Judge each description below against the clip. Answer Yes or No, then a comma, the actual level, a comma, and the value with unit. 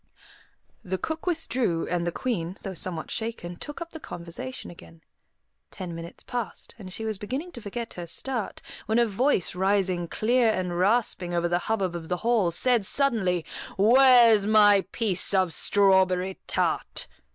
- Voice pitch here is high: Yes, high, 195 Hz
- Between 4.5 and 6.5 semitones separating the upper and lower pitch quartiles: Yes, average, 5.0 semitones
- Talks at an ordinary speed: Yes, average, 160 wpm